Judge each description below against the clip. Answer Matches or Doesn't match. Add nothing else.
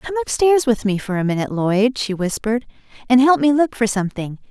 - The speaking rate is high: Matches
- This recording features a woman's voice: Matches